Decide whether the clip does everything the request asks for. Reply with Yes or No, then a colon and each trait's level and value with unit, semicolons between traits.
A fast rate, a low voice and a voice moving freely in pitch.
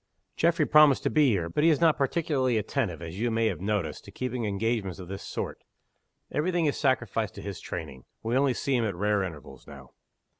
Yes: fast, 215 wpm; low, 115 Hz; wide, 6.4 semitones